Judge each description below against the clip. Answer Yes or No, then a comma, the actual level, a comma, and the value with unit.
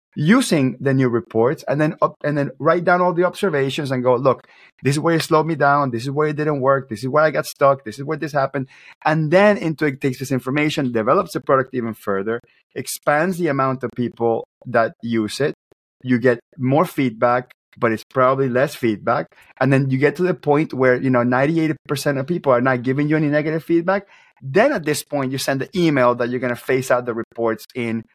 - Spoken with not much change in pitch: No, average, 3.6 semitones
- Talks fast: Yes, fast, 230 wpm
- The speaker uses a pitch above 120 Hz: Yes, low, 135 Hz